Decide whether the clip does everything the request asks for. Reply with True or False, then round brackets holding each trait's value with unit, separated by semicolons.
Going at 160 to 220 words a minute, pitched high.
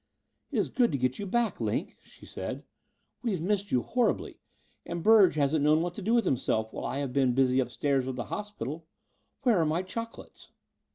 False (205 wpm; 165 Hz)